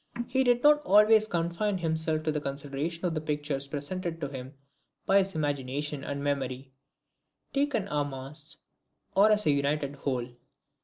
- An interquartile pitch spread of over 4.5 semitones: Yes, average, 5.1 semitones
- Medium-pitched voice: Yes, medium, 150 Hz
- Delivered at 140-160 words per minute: Yes, average, 155 wpm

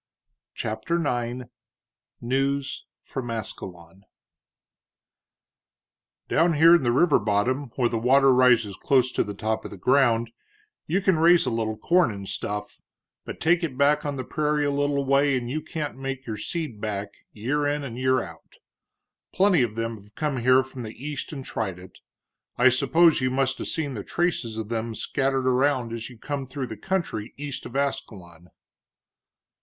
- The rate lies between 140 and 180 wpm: Yes, average, 170 wpm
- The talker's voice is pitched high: No, low, 130 Hz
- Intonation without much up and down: No, average, 4.1 semitones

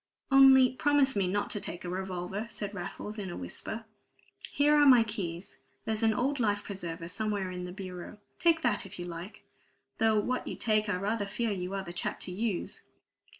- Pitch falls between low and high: No, high, 205 Hz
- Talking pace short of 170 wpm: No, average, 195 wpm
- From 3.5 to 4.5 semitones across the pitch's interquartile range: Yes, average, 4.2 semitones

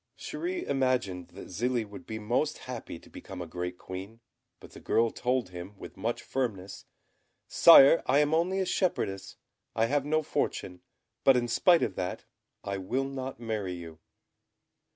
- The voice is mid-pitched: No, low, 115 Hz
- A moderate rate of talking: Yes, average, 165 wpm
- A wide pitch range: Yes, wide, 6.1 semitones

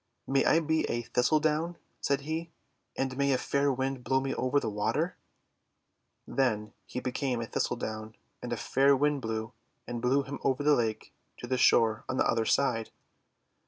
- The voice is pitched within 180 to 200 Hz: No, low, 130 Hz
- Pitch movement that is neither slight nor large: Yes, average, 3.2 semitones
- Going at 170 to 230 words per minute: Yes, average, 180 wpm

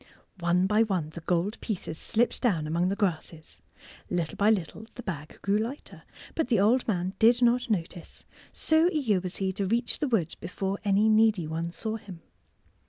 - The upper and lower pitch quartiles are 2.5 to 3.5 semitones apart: No, average, 4.5 semitones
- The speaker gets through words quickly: No, average, 180 wpm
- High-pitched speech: Yes, high, 200 Hz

